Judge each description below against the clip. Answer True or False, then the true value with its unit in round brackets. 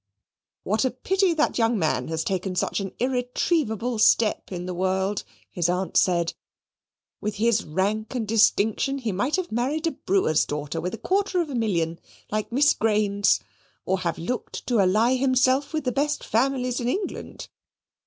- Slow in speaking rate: False (170 wpm)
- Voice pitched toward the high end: True (220 Hz)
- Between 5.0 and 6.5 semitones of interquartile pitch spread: True (5.4 semitones)